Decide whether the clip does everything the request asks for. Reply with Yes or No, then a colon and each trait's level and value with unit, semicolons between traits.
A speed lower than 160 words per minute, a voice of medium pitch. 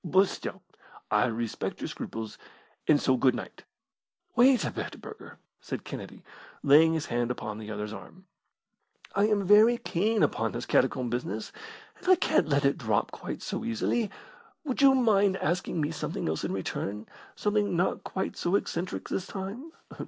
No: average, 165 wpm; medium, 170 Hz